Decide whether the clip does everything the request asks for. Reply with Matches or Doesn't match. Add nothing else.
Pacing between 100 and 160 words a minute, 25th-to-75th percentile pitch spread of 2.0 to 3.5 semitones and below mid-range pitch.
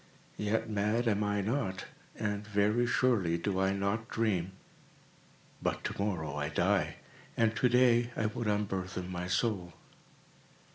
Matches